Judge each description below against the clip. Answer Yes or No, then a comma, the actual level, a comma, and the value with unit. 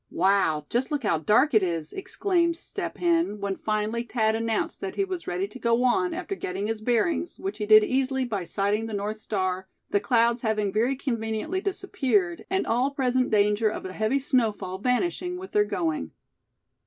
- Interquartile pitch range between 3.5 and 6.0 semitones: Yes, average, 4.9 semitones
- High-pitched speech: Yes, high, 225 Hz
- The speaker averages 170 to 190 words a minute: Yes, average, 185 wpm